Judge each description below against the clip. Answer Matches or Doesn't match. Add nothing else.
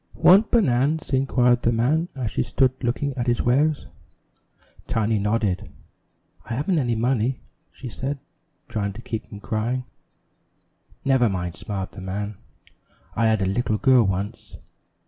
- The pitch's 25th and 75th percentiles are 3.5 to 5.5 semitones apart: Matches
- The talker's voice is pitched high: Doesn't match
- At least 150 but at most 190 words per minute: Doesn't match